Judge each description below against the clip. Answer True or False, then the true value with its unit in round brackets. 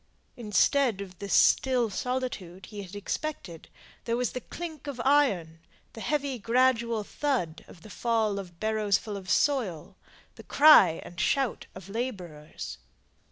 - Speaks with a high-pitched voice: True (220 Hz)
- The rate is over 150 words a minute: False (145 wpm)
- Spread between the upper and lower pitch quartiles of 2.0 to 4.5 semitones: False (5.4 semitones)